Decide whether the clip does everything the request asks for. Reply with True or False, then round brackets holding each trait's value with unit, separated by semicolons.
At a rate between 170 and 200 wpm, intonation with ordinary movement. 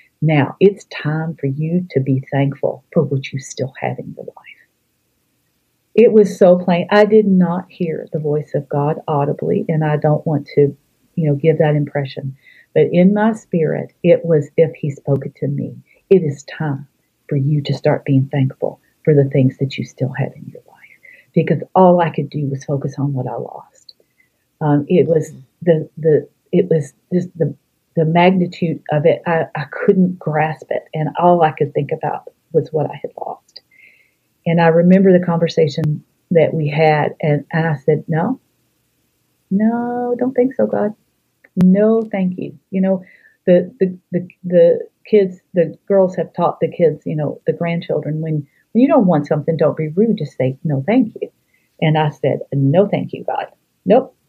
True (190 wpm; 3.8 semitones)